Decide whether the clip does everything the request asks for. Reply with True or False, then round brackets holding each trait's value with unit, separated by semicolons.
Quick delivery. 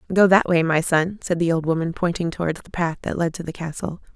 True (260 wpm)